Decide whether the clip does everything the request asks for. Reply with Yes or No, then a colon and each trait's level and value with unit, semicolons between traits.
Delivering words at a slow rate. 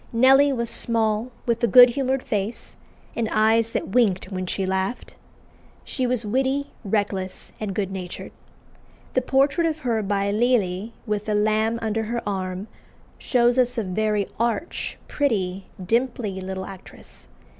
No: average, 145 wpm